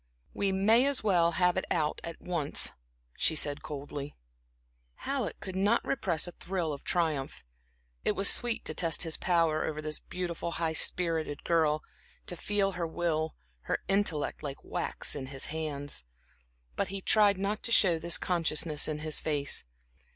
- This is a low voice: No, medium, 170 Hz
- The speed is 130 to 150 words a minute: No, average, 165 wpm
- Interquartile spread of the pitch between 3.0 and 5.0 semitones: Yes, average, 3.7 semitones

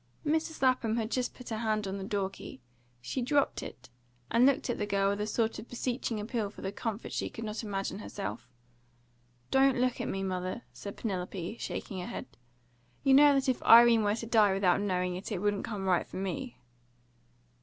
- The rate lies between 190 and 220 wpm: Yes, average, 200 wpm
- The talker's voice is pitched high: Yes, high, 215 Hz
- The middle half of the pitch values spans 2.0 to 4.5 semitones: Yes, average, 3.9 semitones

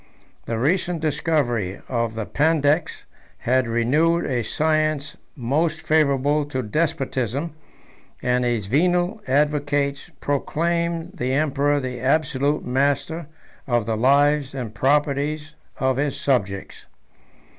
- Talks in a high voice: No, medium, 145 Hz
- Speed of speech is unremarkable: No, slow, 110 wpm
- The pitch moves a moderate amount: Yes, average, 3.4 semitones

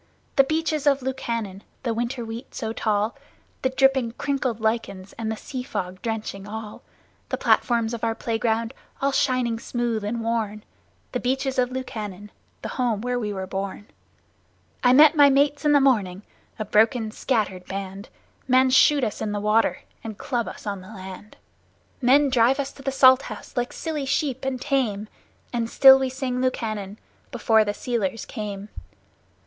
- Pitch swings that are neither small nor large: Yes, average, 3.8 semitones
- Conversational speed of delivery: Yes, average, 170 wpm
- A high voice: Yes, high, 235 Hz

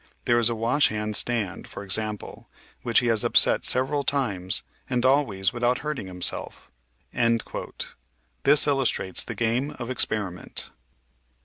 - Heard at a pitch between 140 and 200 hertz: No, low, 120 Hz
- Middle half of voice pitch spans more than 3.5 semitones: Yes, average, 4.2 semitones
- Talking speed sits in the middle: No, slow, 130 wpm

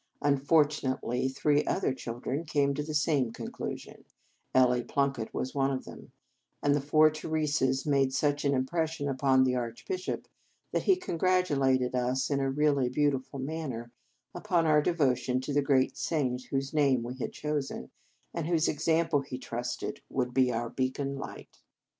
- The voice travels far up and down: No, average, 2.7 semitones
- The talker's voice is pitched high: No, medium, 140 Hz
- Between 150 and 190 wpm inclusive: Yes, average, 160 wpm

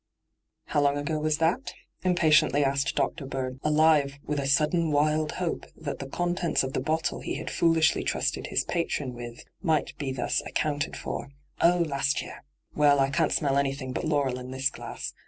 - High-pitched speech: No, medium, 145 Hz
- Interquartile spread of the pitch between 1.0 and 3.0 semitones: Yes, narrow, 2.6 semitones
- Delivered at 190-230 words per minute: Yes, average, 200 wpm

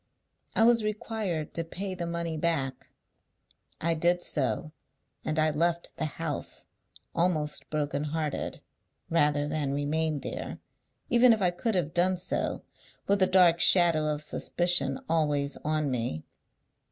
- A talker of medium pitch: Yes, medium, 160 Hz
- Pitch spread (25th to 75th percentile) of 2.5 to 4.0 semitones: Yes, average, 3.0 semitones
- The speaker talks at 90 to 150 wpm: Yes, average, 140 wpm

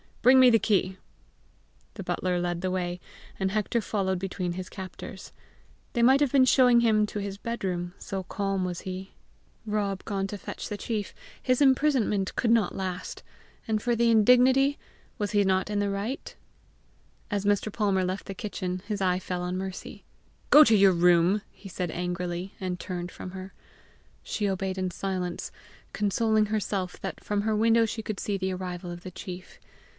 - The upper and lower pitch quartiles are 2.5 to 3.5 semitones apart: Yes, average, 2.8 semitones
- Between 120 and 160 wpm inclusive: No, average, 180 wpm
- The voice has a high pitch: Yes, high, 195 Hz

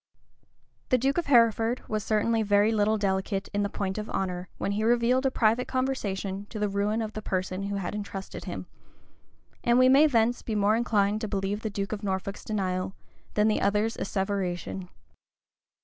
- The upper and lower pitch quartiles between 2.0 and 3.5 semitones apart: Yes, narrow, 2.4 semitones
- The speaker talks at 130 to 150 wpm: No, average, 185 wpm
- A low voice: No, high, 210 Hz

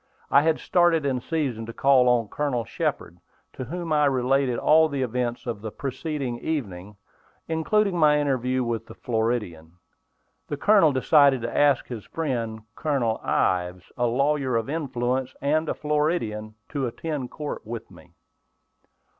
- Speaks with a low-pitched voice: Yes, low, 130 Hz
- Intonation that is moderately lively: Yes, average, 4.3 semitones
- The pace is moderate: Yes, average, 150 wpm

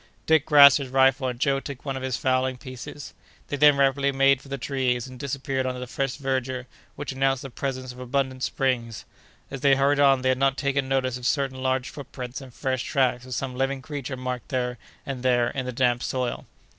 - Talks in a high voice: No, low, 130 Hz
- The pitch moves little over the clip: Yes, narrow, 1.3 semitones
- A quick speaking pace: Yes, fast, 215 wpm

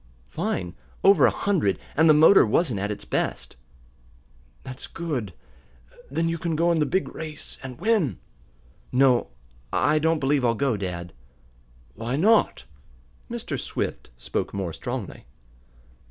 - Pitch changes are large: Yes, wide, 7.1 semitones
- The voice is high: No, medium, 140 Hz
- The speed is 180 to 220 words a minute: No, average, 140 wpm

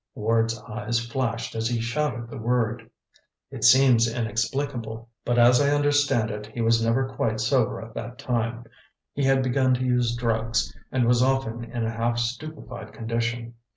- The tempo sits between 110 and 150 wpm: No, average, 165 wpm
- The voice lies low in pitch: Yes, low, 120 Hz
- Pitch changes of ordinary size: No, narrow, 2.1 semitones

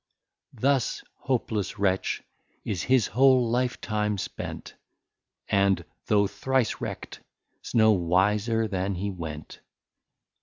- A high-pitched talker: No, low, 105 Hz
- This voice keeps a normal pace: No, slow, 110 wpm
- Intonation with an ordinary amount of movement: Yes, average, 3.8 semitones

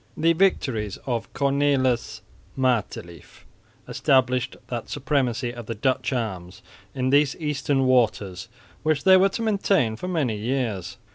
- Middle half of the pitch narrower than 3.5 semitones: No, average, 4.0 semitones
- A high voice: No, low, 130 Hz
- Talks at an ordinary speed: No, slow, 130 wpm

